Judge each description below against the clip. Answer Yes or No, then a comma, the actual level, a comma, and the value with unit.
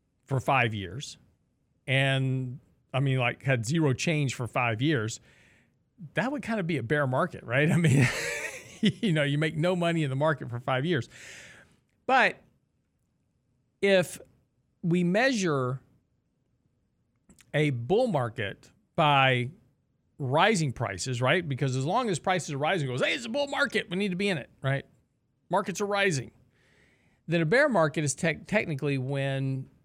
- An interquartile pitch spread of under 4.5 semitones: No, average, 4.8 semitones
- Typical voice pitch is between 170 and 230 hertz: No, medium, 140 Hz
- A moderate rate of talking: Yes, average, 160 wpm